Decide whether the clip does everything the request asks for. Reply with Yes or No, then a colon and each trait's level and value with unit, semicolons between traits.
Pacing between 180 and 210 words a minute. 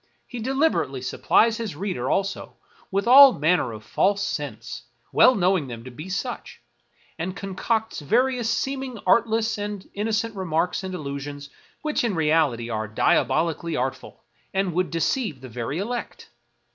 No: average, 145 wpm